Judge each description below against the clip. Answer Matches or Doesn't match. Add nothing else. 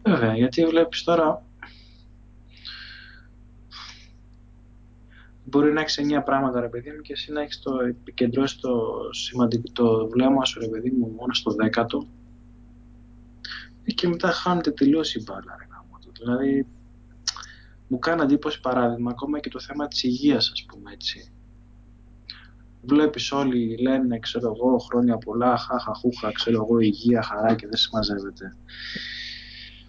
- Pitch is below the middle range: Matches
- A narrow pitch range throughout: Matches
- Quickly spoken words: Doesn't match